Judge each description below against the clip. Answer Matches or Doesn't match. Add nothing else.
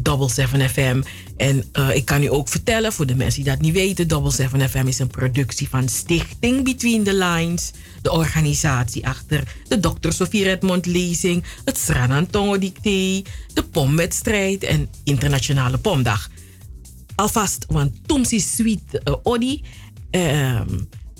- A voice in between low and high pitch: Matches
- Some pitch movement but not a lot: Doesn't match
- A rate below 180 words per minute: Matches